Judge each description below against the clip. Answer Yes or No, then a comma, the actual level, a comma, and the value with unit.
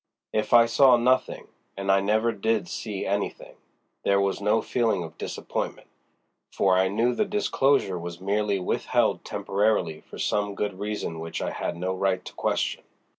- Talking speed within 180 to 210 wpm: No, average, 155 wpm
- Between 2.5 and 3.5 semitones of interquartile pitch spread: Yes, average, 3.0 semitones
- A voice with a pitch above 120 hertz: No, low, 100 Hz